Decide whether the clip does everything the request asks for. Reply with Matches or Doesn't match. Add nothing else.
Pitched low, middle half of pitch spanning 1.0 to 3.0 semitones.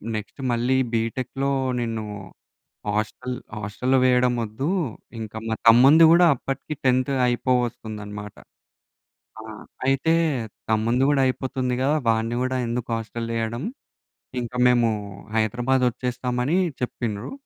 Matches